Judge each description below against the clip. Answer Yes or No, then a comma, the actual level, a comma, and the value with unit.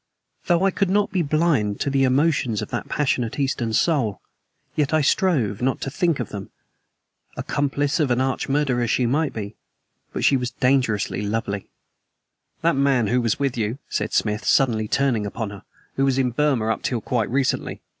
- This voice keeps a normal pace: Yes, average, 180 wpm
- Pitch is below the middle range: Yes, low, 130 Hz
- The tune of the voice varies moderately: Yes, average, 4.4 semitones